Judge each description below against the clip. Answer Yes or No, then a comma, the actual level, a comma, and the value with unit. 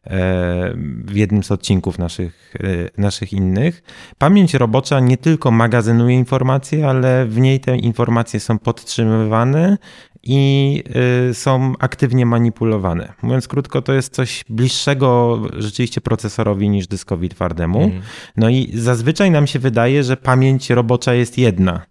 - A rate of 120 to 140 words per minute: Yes, average, 125 wpm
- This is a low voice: Yes, low, 120 Hz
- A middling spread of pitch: Yes, average, 3.8 semitones